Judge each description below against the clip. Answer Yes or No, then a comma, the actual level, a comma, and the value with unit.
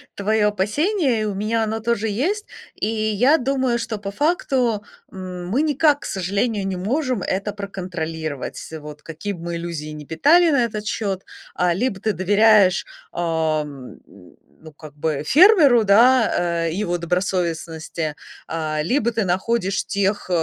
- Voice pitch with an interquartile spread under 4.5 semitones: No, wide, 5.4 semitones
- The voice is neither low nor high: No, high, 200 Hz